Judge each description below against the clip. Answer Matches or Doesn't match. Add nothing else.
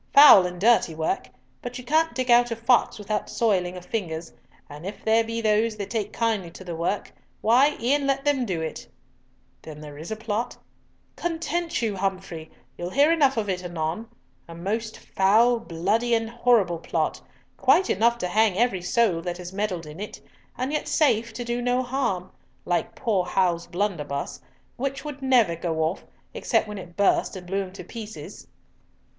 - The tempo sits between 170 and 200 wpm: Matches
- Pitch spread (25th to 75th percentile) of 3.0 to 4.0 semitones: Doesn't match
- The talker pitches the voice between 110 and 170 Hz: Doesn't match